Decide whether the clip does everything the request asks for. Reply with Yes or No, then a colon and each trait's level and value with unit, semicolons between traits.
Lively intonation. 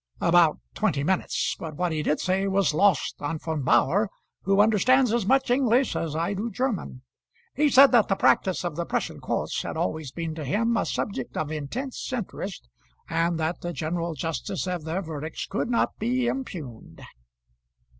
Yes: wide, 6.1 semitones